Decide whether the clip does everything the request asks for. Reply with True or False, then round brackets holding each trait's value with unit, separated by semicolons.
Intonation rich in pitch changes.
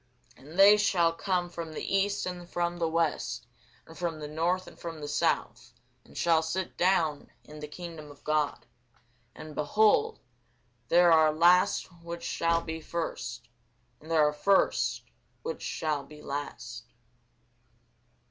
False (2.6 semitones)